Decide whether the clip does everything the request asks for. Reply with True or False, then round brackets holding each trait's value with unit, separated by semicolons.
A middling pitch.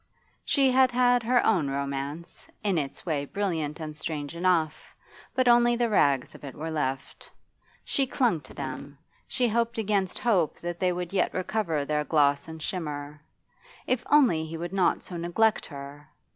True (170 Hz)